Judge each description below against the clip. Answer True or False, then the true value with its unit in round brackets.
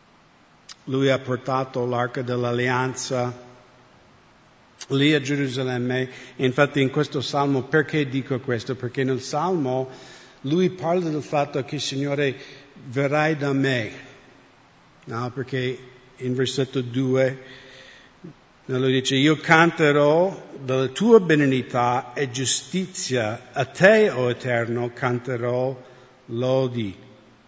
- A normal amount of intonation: False (2.2 semitones)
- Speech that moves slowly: True (105 wpm)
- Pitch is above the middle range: False (130 Hz)